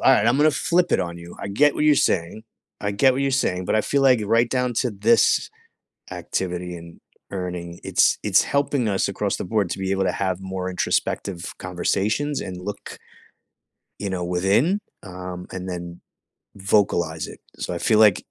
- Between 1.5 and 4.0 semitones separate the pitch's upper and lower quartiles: No, average, 5.0 semitones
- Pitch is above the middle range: No, low, 100 Hz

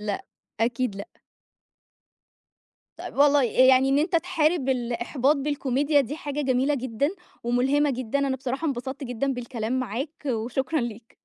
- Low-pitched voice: No, very high, 265 Hz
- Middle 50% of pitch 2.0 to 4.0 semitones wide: Yes, average, 3.0 semitones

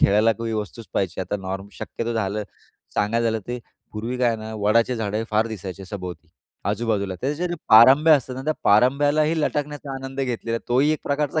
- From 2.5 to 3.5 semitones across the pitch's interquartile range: No, average, 4.3 semitones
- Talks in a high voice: No, low, 115 Hz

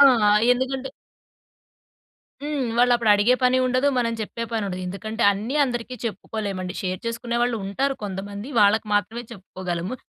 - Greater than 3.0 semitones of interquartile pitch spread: Yes, average, 3.7 semitones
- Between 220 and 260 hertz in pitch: Yes, high, 225 Hz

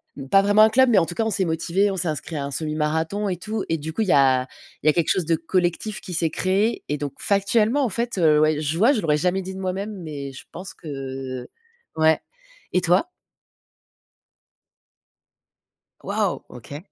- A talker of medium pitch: Yes, medium, 175 Hz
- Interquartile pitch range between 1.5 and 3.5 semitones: No, average, 4.8 semitones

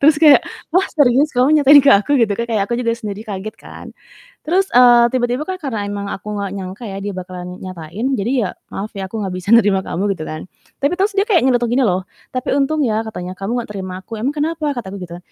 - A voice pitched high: Yes, high, 225 Hz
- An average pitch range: No, wide, 5.9 semitones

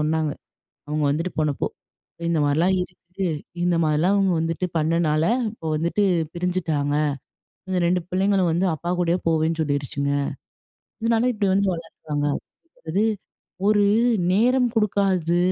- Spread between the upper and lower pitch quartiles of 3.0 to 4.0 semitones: Yes, average, 3.6 semitones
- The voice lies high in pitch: No, medium, 170 Hz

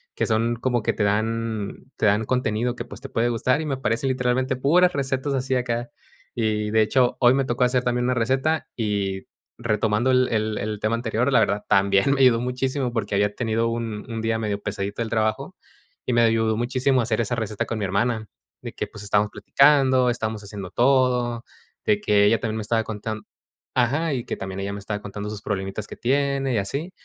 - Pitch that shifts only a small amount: No, average, 3.1 semitones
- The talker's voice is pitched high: No, low, 115 Hz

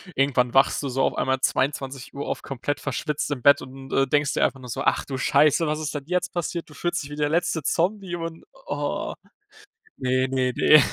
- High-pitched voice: No, medium, 145 Hz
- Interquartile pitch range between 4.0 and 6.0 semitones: No, average, 2.8 semitones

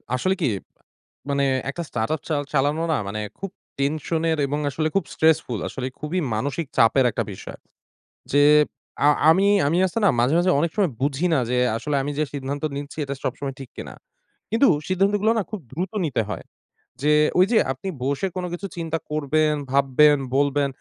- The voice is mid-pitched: Yes, medium, 150 Hz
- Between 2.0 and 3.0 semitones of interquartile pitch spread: No, average, 3.7 semitones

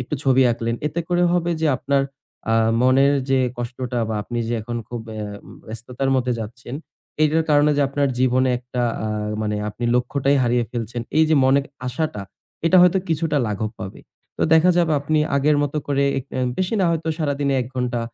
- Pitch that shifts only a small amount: No, average, 3.7 semitones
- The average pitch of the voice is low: Yes, low, 130 Hz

